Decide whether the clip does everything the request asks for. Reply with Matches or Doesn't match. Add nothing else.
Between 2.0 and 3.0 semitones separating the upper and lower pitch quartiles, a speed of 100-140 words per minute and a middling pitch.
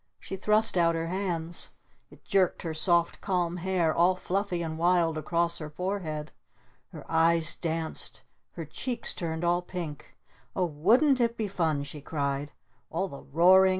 Doesn't match